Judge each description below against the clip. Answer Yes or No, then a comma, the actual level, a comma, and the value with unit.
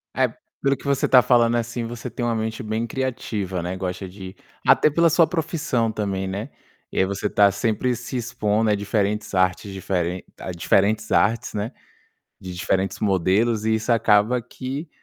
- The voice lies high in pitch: No, low, 110 Hz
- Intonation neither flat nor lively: Yes, average, 3.7 semitones